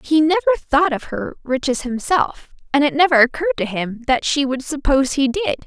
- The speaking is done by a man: No, female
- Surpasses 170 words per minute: Yes, average, 200 wpm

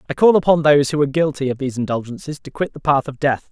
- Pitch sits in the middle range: Yes, medium, 145 Hz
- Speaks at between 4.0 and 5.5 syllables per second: No, 7.2 syllables/s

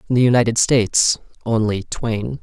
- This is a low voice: Yes, low, 115 Hz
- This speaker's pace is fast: No, average, 150 wpm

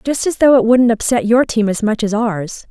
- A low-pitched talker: No, high, 230 Hz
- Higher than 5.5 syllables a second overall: No, 5.0 syllables/s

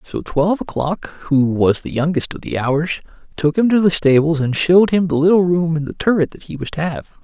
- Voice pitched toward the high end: No, medium, 165 Hz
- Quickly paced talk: Yes, fast, 240 wpm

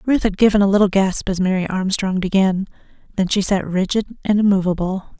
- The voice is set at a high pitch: Yes, high, 195 Hz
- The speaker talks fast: No, average, 185 wpm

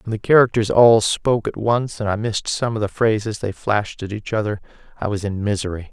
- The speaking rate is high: Yes, fast, 235 wpm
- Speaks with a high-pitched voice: No, low, 105 Hz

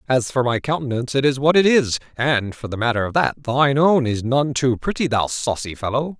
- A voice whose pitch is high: No, low, 130 Hz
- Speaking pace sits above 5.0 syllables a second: Yes, 5.5 syllables/s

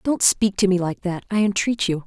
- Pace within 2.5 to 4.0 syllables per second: No, 5.2 syllables/s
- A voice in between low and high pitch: No, high, 195 Hz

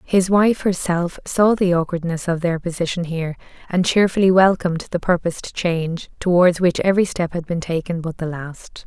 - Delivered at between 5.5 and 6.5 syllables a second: No, 5.2 syllables/s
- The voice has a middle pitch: Yes, medium, 175 Hz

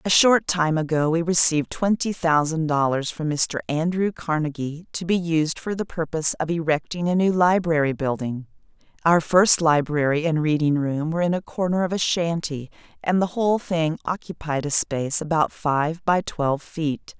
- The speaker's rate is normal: Yes, average, 175 wpm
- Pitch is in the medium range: Yes, medium, 160 Hz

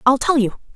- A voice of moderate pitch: No, very high, 260 Hz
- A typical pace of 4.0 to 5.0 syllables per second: No, 5.9 syllables/s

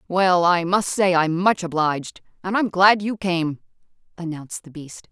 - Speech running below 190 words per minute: Yes, average, 175 wpm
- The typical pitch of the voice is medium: Yes, medium, 175 Hz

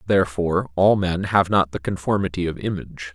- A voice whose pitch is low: Yes, very low, 90 Hz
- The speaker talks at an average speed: Yes, average, 170 wpm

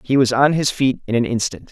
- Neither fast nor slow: No, fast, 280 wpm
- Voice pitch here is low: Yes, low, 130 Hz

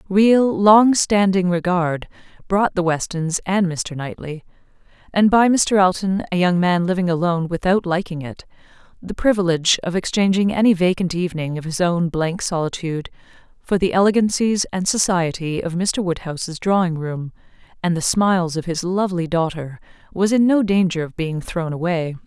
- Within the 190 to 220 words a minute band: No, average, 155 wpm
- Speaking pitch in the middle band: Yes, medium, 180 Hz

